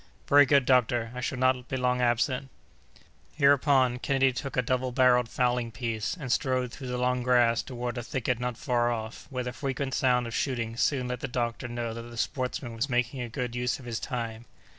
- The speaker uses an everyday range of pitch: No, narrow, 1.5 semitones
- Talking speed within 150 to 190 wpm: No, fast, 205 wpm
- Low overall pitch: Yes, low, 125 Hz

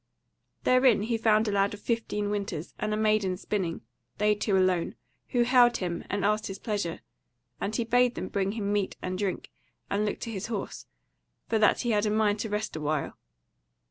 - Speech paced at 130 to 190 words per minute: No, average, 200 wpm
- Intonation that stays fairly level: Yes, narrow, 2.1 semitones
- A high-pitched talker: Yes, high, 210 Hz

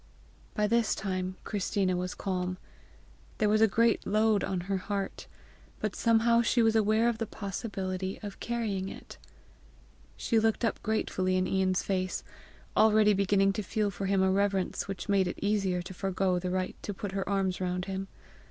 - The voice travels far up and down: No, narrow, 2.4 semitones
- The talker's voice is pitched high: Yes, high, 195 Hz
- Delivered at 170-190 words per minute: Yes, average, 175 wpm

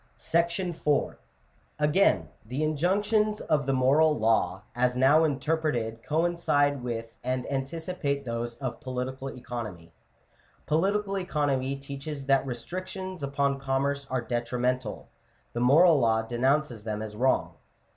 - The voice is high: No, low, 135 Hz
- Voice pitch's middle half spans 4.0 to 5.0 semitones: Yes, average, 4.3 semitones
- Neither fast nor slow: No, slow, 125 wpm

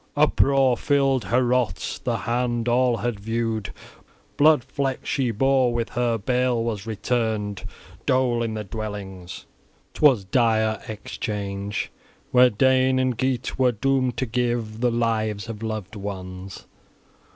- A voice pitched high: No, low, 115 Hz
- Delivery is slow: Yes, slow, 130 wpm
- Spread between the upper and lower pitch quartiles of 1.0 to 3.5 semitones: Yes, average, 3.0 semitones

